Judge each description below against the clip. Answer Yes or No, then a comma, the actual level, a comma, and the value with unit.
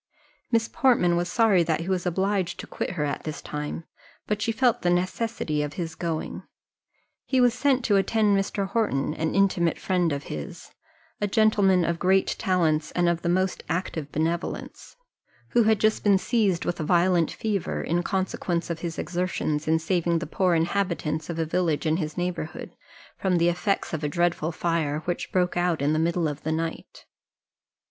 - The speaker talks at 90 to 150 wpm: No, average, 185 wpm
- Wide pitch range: No, average, 3.2 semitones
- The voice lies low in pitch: No, medium, 175 Hz